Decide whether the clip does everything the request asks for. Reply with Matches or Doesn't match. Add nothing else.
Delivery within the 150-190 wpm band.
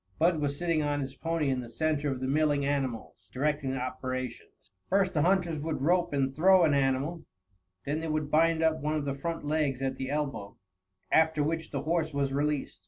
Doesn't match